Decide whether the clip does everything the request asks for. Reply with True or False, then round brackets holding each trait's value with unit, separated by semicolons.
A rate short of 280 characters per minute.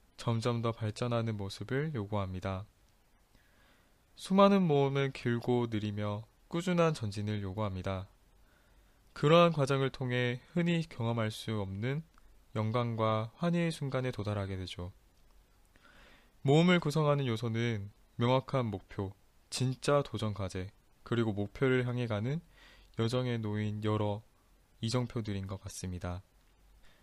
True (260 characters per minute)